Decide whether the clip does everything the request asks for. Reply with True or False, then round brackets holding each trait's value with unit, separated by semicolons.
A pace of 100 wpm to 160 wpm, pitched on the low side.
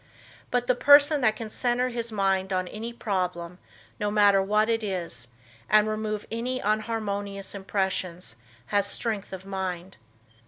False (145 wpm; 205 Hz)